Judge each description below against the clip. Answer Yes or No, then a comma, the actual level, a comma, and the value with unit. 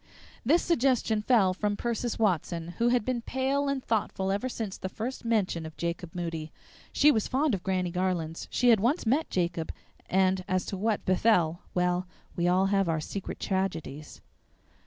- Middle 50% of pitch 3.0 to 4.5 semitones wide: No, average, 4.9 semitones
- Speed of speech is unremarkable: Yes, average, 175 wpm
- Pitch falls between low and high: No, high, 195 Hz